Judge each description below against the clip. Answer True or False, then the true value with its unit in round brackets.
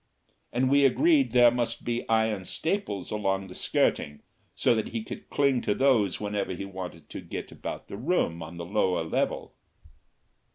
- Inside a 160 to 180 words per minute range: True (170 wpm)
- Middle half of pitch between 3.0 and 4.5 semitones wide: False (5.0 semitones)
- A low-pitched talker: True (110 Hz)